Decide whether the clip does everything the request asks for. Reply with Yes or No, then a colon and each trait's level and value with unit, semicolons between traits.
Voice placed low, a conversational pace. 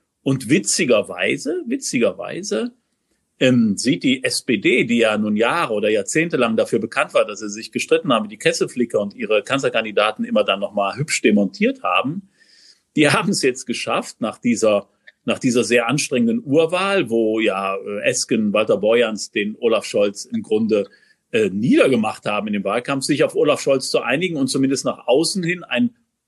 Yes: low, 125 Hz; average, 170 wpm